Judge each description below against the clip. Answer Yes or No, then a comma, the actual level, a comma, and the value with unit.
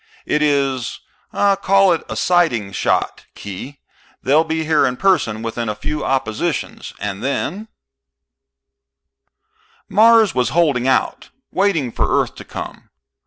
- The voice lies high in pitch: No, medium, 140 Hz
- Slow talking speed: Yes, slow, 130 wpm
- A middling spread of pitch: No, wide, 7.1 semitones